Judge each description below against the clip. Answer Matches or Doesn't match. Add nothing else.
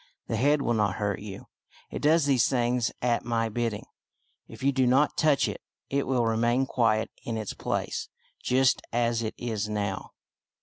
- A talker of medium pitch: Doesn't match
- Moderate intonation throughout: Matches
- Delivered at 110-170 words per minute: Doesn't match